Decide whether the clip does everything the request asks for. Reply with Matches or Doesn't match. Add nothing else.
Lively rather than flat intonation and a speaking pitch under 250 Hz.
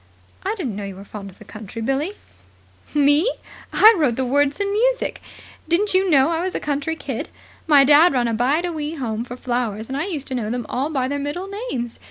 Doesn't match